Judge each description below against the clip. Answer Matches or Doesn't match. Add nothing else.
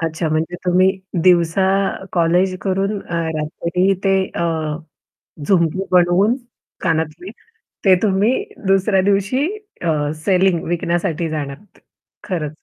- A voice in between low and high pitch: Matches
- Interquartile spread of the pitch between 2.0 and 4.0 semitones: Matches